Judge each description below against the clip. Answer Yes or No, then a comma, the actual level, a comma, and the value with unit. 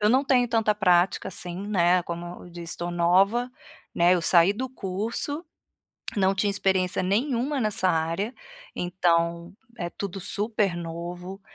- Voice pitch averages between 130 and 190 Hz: Yes, medium, 185 Hz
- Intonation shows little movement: No, average, 3.4 semitones